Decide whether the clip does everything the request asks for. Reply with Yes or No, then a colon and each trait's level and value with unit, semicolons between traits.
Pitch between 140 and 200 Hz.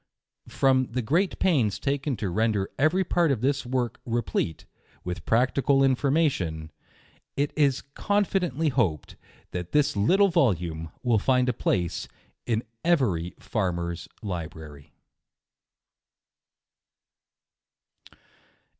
No: low, 125 Hz